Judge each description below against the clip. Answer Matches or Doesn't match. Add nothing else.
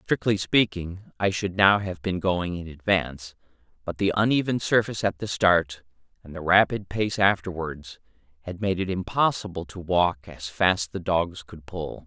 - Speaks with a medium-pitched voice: Doesn't match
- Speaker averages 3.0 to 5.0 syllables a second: Matches